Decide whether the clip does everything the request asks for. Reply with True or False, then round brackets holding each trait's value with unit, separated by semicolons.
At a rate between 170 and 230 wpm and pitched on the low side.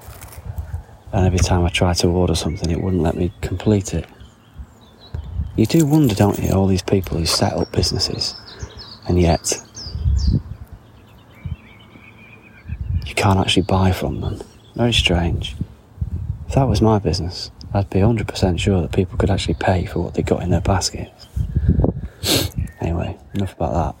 False (155 wpm; 95 Hz)